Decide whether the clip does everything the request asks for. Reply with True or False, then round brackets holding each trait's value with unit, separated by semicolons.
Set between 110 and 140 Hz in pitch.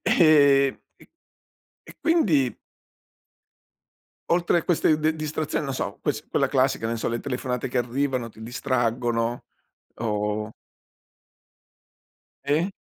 True (135 Hz)